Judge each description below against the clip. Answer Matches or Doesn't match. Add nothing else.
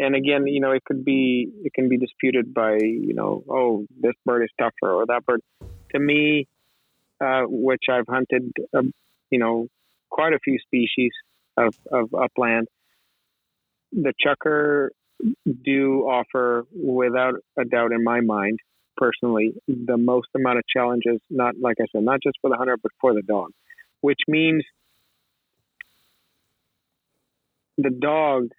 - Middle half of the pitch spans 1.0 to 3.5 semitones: Matches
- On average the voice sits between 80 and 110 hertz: Doesn't match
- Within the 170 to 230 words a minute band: Doesn't match